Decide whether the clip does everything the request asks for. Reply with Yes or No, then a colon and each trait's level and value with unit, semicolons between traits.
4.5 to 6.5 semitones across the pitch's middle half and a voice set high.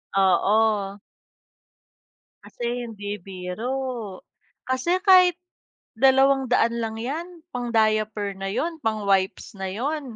Yes: average, 4.8 semitones; high, 225 Hz